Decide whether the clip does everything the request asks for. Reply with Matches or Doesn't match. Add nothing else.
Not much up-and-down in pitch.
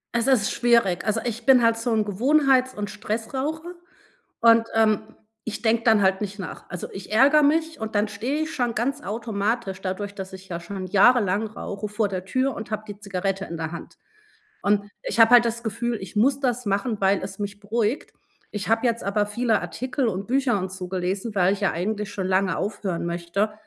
Doesn't match